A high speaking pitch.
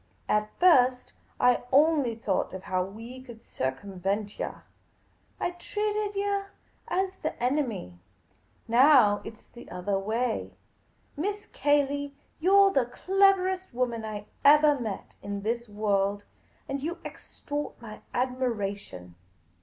Yes: very high, 250 Hz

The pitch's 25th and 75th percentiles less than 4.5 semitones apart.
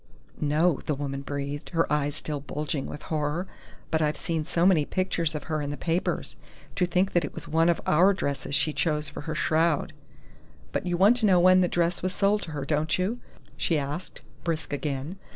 Yes: average, 3.3 semitones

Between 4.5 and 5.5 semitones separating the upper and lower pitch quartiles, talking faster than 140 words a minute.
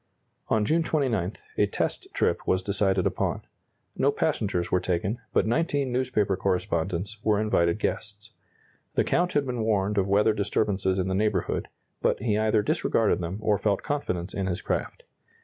No: average, 2.7 semitones; average, 165 wpm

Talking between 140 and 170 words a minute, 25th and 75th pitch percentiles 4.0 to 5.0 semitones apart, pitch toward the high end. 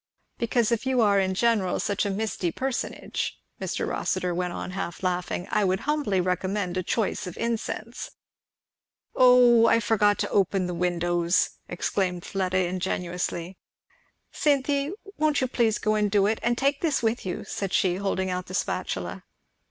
Yes: average, 160 wpm; average, 4.3 semitones; high, 200 Hz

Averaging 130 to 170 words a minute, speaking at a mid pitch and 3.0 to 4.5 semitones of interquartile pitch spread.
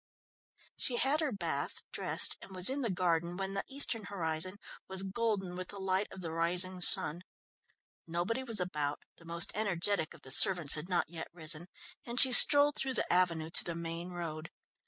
No: average, 185 wpm; medium, 180 Hz; average, 3.4 semitones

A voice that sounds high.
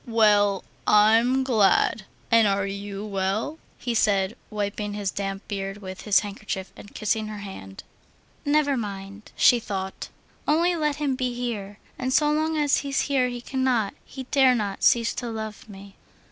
Yes: high, 215 Hz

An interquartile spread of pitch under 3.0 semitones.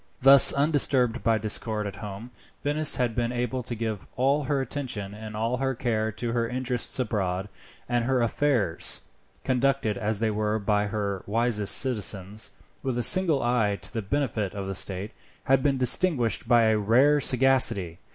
No: average, 3.7 semitones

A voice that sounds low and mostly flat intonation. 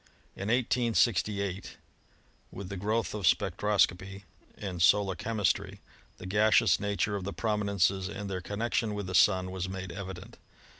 Yes: low, 100 Hz; narrow, 2.0 semitones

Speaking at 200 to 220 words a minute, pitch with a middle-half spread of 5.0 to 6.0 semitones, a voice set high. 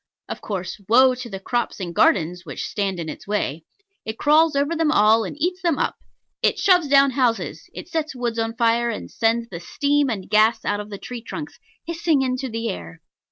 Yes: fast, 205 wpm; wide, 5.5 semitones; high, 235 Hz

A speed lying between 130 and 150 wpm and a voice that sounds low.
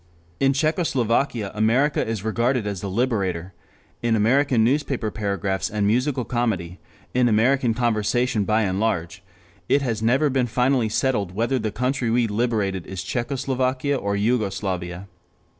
Yes: average, 140 wpm; low, 115 Hz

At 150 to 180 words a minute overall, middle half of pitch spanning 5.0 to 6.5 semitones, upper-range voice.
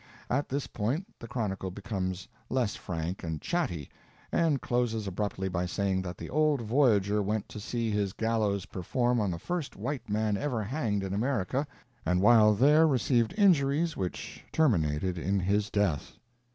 No: average, 160 wpm; average, 5.3 semitones; low, 105 Hz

